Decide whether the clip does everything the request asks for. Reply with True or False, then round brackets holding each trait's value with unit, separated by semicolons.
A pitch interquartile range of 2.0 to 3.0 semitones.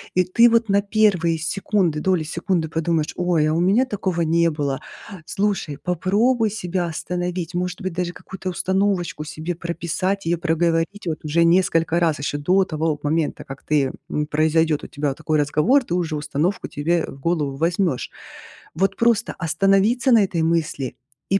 False (3.5 semitones)